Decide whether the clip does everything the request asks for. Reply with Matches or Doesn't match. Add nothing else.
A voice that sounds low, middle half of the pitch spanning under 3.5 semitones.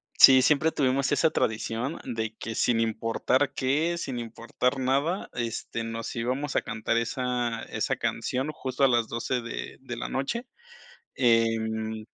Matches